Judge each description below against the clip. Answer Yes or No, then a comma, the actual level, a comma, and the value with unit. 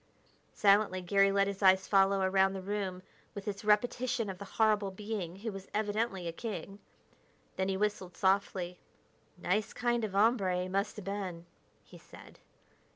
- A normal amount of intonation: No, narrow, 1.8 semitones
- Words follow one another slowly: No, average, 160 wpm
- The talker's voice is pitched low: No, high, 195 Hz